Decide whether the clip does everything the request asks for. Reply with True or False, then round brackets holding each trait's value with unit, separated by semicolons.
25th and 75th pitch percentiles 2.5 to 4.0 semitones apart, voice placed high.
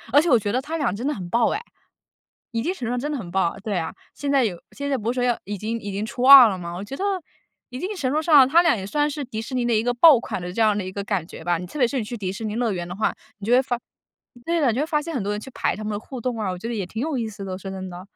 False (5.3 semitones; 230 Hz)